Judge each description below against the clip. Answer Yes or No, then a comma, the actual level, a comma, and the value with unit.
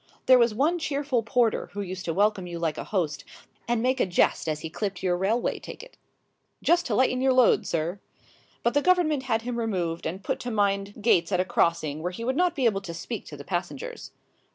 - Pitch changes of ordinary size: No, wide, 6.2 semitones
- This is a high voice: Yes, high, 210 Hz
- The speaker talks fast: Yes, fast, 225 wpm